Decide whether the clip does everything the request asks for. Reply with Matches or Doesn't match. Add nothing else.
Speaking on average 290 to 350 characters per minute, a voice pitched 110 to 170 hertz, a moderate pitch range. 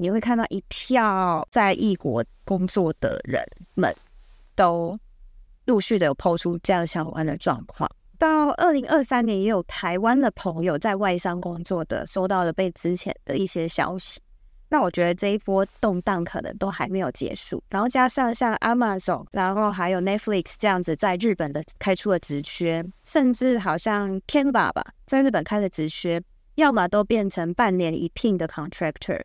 Doesn't match